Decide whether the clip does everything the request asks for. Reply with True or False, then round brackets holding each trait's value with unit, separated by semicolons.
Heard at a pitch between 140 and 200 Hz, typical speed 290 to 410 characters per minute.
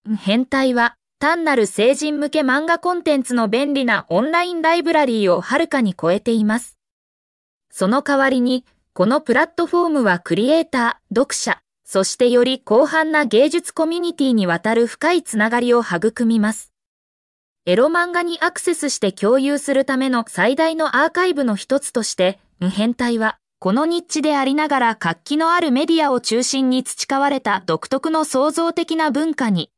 False (265 Hz; 345 characters per minute)